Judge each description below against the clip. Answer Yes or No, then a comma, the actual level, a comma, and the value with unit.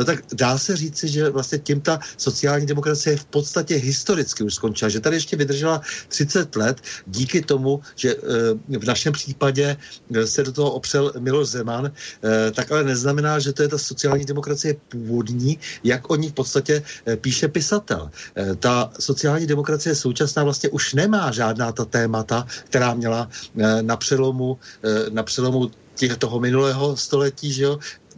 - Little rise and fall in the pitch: No, average, 3.5 semitones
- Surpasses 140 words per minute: Yes, average, 155 wpm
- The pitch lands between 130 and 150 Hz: Yes, medium, 140 Hz